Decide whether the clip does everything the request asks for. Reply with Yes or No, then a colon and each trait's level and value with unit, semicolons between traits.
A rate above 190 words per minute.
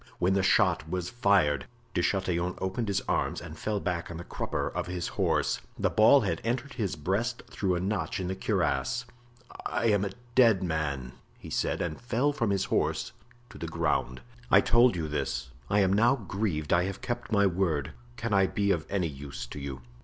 Yes: average, 200 wpm